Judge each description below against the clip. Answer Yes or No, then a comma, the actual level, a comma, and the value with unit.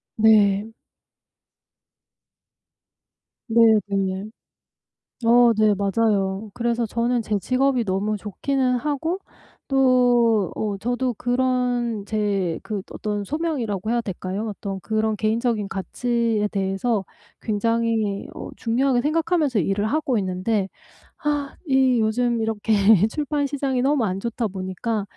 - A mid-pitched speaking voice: No, high, 225 Hz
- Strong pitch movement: No, average, 3.5 semitones